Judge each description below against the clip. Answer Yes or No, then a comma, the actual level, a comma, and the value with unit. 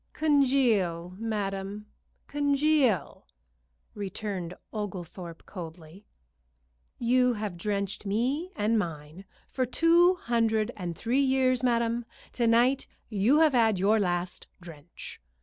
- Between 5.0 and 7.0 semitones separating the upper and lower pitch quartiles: Yes, wide, 5.5 semitones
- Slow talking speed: Yes, slow, 105 wpm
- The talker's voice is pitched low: No, high, 215 Hz